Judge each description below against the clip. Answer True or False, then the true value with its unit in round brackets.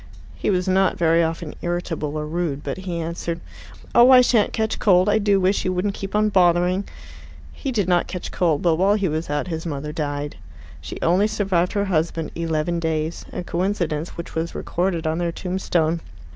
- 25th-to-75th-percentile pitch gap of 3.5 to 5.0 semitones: False (2.9 semitones)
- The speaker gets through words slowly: False (190 wpm)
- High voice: False (175 Hz)